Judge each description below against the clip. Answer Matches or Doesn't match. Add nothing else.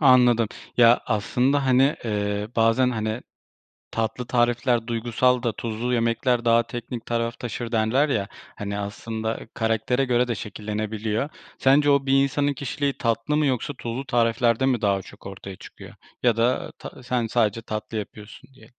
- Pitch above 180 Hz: Doesn't match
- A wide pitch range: Doesn't match